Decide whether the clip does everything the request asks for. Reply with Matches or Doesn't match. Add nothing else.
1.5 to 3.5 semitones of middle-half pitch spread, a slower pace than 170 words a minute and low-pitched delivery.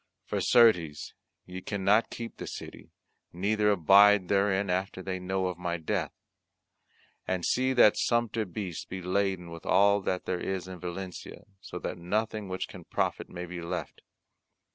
Matches